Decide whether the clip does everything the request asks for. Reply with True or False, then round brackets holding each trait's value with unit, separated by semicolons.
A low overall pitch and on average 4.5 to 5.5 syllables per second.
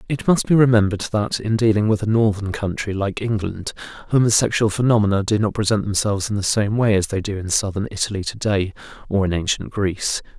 False (105 Hz; 6.1 syllables/s)